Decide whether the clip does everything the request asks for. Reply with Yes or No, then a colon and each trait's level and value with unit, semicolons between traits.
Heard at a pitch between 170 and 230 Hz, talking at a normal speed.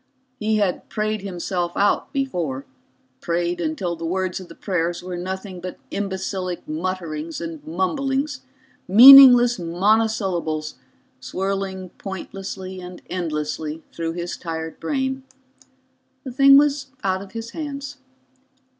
No: high, 190 Hz; slow, 120 wpm